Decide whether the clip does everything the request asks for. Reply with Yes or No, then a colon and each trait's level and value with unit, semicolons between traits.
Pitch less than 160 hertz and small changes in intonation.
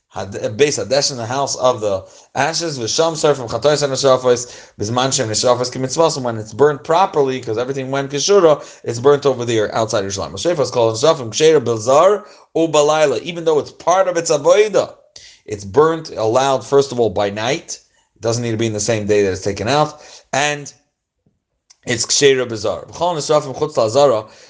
No: low, 135 Hz; average, 4.6 semitones